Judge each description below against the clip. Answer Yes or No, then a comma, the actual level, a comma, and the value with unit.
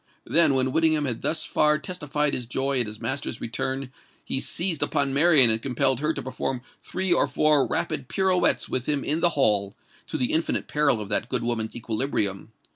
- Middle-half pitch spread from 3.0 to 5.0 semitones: Yes, average, 4.1 semitones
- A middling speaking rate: Yes, average, 190 wpm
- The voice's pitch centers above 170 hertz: No, low, 135 Hz